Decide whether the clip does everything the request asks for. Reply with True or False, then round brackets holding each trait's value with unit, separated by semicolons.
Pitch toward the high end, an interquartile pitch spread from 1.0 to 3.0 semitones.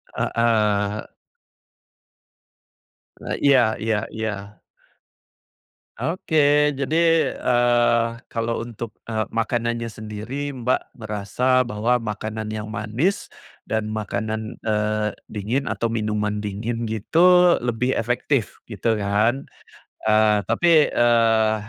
False (115 Hz; 2.5 semitones)